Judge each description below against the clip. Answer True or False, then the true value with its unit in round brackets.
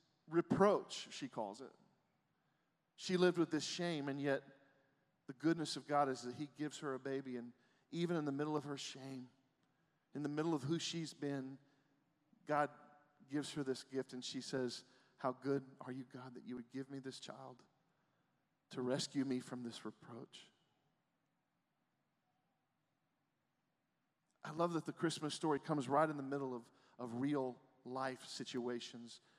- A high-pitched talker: False (140 Hz)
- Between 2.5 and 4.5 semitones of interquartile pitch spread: True (2.8 semitones)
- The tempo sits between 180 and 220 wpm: False (160 wpm)